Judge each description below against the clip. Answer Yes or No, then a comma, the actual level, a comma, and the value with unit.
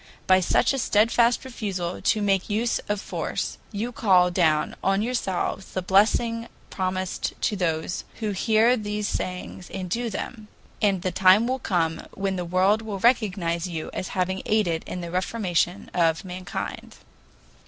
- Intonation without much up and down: No, average, 3.2 semitones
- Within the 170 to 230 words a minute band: No, average, 155 wpm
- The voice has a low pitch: No, high, 190 Hz